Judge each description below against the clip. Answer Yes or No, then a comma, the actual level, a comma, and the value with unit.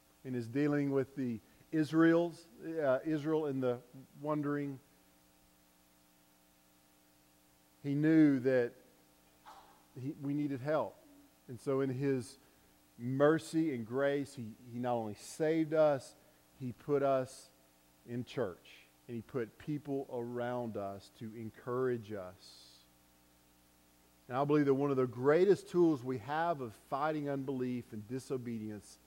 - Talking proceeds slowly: Yes, slow, 125 wpm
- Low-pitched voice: Yes, low, 125 Hz